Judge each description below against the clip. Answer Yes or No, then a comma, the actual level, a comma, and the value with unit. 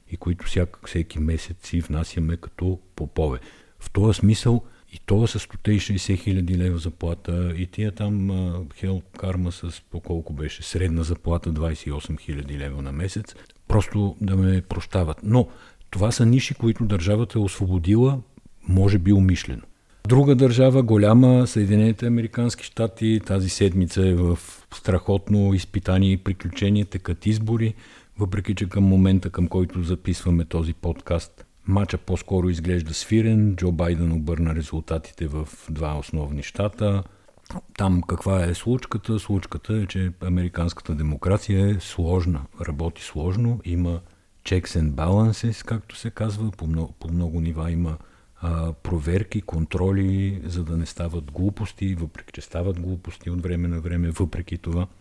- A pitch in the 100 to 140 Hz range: No, very low, 90 Hz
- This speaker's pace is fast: No, average, 145 wpm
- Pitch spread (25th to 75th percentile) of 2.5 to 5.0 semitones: Yes, average, 3.3 semitones